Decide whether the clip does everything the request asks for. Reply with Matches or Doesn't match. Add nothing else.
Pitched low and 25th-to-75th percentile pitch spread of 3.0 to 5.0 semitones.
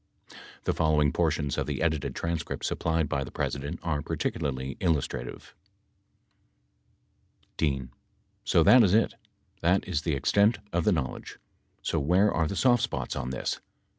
Matches